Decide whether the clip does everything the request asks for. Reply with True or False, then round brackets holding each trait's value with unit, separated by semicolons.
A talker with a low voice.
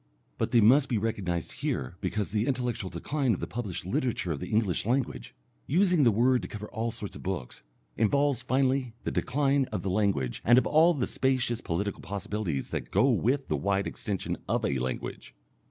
True (115 Hz)